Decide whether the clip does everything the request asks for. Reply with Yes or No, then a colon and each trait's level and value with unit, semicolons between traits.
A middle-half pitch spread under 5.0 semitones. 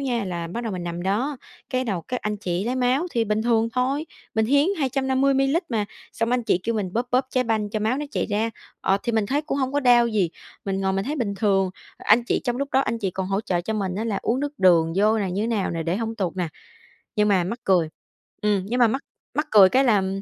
Yes: average, 4.6 semitones